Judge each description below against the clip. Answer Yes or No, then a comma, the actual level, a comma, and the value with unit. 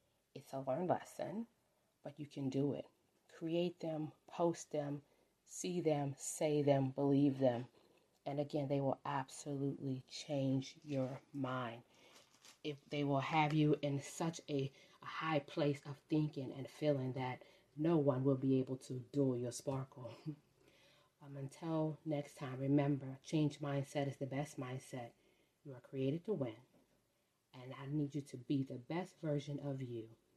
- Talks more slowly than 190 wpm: Yes, average, 155 wpm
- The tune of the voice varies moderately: No, narrow, 2.1 semitones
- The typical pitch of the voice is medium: Yes, medium, 145 Hz